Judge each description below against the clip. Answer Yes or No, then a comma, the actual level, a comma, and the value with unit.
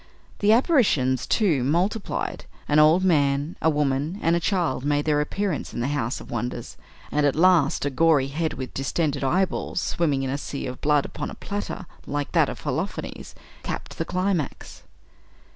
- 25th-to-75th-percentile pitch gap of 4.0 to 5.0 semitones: Yes, average, 4.3 semitones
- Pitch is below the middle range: No, medium, 150 Hz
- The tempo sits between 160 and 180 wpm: Yes, average, 175 wpm